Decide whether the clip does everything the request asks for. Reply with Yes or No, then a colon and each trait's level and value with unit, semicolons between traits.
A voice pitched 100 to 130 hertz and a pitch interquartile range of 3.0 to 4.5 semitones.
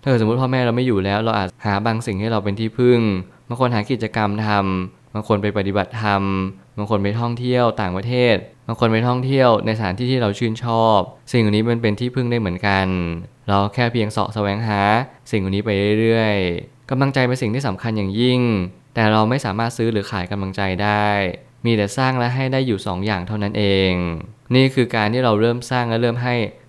Yes: low, 110 Hz; average, 3.3 semitones